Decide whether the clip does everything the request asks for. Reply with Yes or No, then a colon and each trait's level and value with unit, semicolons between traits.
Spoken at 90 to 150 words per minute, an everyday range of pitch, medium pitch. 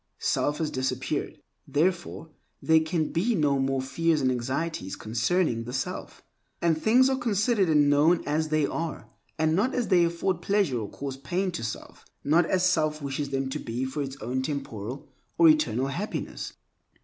No: average, 175 wpm; average, 4.5 semitones; medium, 155 Hz